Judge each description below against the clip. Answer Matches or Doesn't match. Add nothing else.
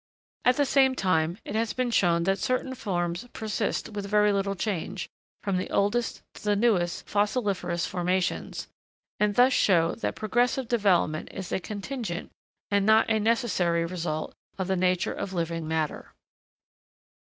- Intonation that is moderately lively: Matches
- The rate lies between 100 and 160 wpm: Matches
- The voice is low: Doesn't match